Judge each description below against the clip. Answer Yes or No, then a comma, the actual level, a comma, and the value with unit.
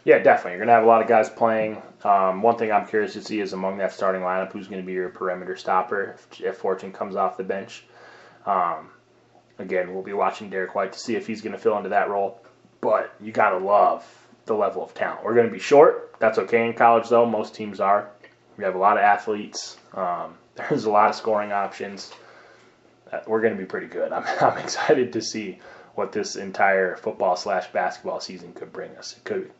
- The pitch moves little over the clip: No, average, 3.3 semitones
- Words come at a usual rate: No, fast, 230 wpm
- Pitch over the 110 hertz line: No, low, 105 Hz